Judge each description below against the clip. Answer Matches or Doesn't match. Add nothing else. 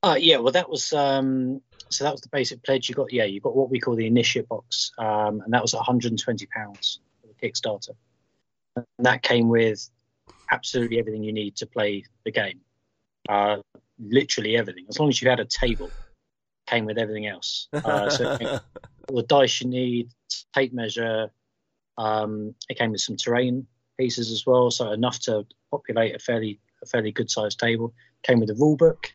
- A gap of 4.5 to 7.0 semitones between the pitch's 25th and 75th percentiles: Doesn't match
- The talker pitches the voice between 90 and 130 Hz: Matches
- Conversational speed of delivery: Matches